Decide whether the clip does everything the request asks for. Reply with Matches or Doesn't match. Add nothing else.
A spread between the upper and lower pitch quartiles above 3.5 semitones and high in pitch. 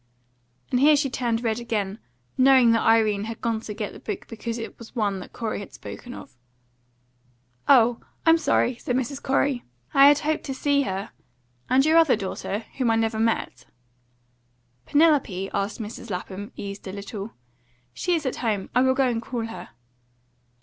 Matches